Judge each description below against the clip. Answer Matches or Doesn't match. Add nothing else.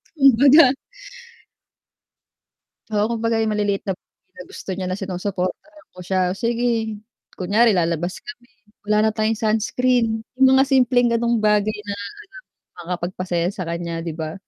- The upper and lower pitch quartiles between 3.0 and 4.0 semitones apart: Doesn't match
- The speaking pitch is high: Matches